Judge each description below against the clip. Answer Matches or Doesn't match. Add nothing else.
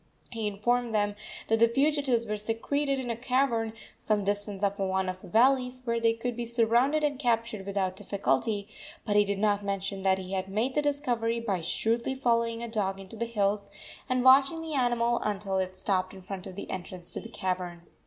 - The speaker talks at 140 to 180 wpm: Doesn't match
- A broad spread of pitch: Doesn't match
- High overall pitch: Matches